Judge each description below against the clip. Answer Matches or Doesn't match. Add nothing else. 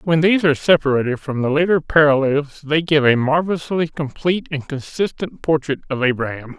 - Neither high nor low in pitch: Matches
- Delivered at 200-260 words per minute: Doesn't match